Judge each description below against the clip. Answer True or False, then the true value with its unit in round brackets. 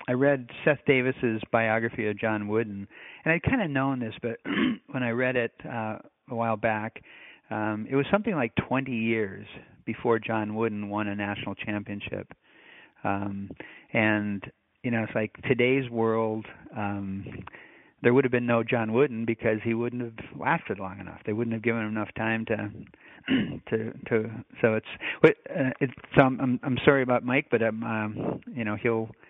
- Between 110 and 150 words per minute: False (175 wpm)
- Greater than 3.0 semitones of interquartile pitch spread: False (2.7 semitones)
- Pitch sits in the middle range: False (115 Hz)